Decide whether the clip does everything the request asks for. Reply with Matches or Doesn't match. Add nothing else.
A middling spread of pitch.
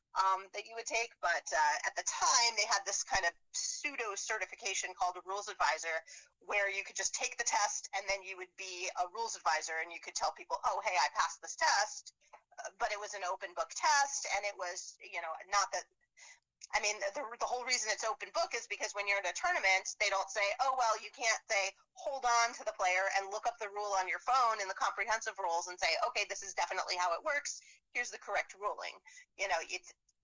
Matches